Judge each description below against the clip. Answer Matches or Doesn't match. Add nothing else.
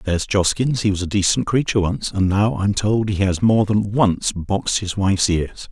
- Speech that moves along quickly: Matches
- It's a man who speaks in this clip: Matches